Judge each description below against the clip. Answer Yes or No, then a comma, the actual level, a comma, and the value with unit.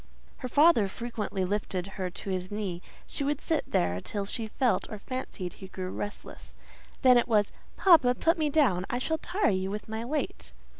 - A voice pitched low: No, high, 215 Hz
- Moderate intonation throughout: No, wide, 6.3 semitones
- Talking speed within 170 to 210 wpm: Yes, average, 185 wpm